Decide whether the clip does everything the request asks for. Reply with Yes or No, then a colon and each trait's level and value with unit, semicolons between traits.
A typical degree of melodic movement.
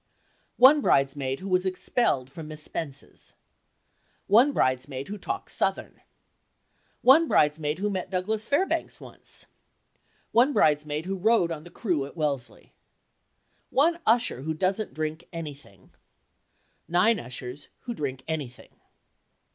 No: wide, 6.9 semitones